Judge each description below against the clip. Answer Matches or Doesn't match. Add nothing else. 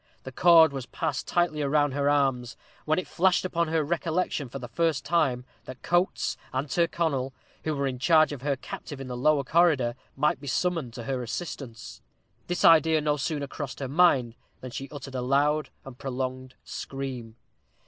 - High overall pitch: Doesn't match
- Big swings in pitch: Doesn't match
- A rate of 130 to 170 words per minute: Doesn't match